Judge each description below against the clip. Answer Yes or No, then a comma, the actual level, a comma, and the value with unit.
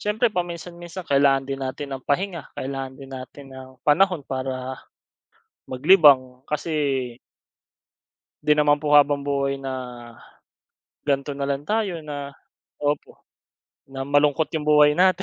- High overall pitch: No, medium, 145 Hz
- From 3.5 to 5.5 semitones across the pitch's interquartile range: No, average, 2.8 semitones